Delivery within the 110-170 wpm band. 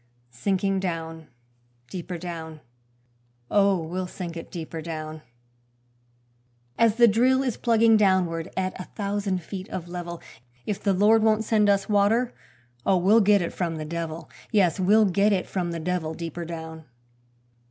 Yes: average, 150 wpm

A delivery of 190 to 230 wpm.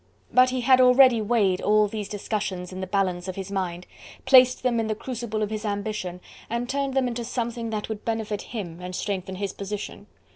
Yes: fast, 205 wpm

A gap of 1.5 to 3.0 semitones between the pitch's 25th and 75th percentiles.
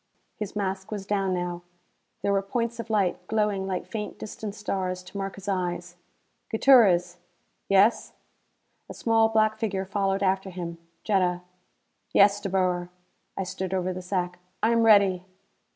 Yes: narrow, 2.4 semitones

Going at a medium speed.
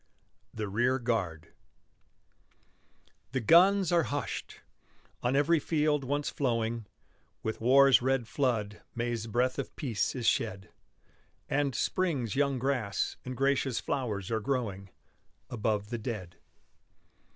No: slow, 120 wpm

